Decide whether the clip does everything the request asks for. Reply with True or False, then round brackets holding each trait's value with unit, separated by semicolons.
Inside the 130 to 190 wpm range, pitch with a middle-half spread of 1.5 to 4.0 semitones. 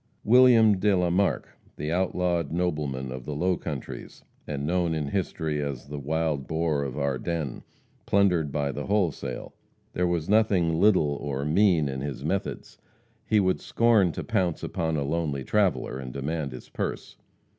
False (160 wpm; 4.4 semitones)